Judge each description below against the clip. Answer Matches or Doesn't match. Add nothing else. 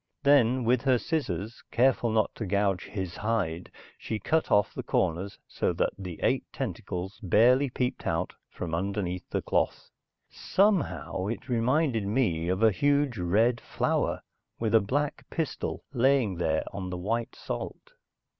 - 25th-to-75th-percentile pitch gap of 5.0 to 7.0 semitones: Matches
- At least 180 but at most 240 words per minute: Doesn't match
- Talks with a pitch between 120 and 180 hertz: Doesn't match